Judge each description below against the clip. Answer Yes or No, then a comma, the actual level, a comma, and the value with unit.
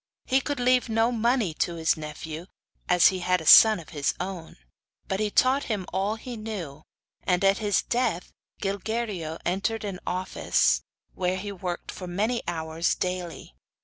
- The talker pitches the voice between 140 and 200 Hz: Yes, high, 190 Hz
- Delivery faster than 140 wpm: Yes, average, 165 wpm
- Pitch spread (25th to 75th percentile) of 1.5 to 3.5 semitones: No, average, 4.2 semitones